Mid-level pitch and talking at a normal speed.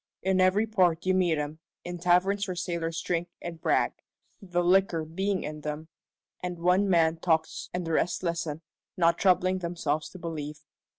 Yes: medium, 175 Hz; average, 170 wpm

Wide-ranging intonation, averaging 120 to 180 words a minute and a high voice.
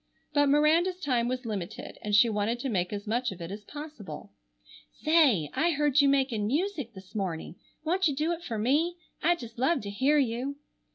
No: wide, 6.3 semitones; average, 195 wpm; very high, 255 Hz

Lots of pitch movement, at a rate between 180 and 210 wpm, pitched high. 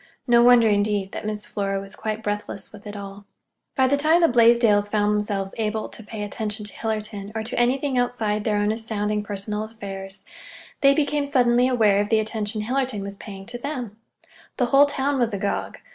No: average, 2.9 semitones; average, 190 wpm; high, 215 Hz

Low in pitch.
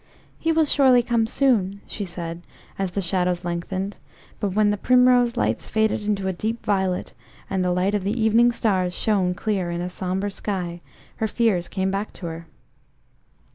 No: high, 195 Hz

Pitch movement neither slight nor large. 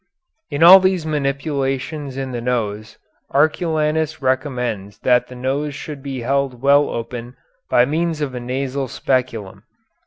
Yes: average, 3.2 semitones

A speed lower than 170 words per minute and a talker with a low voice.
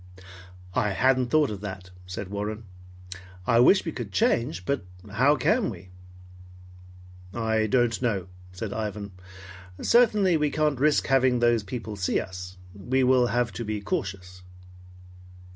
Yes: average, 140 wpm; low, 115 Hz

